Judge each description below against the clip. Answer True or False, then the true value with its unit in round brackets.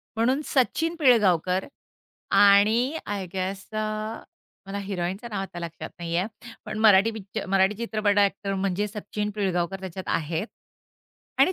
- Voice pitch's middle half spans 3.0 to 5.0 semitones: False (2.4 semitones)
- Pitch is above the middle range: True (200 Hz)